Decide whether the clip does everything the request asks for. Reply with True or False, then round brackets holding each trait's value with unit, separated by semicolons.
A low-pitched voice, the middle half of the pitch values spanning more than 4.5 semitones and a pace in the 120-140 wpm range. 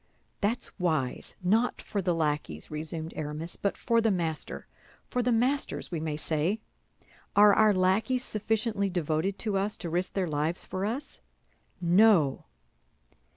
False (185 Hz; 5.3 semitones; 135 wpm)